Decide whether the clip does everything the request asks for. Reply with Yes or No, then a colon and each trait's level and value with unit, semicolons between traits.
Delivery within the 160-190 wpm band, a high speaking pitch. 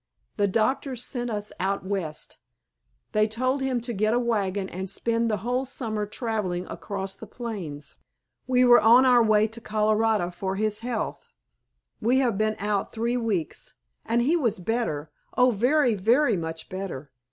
Yes: average, 165 wpm; high, 215 Hz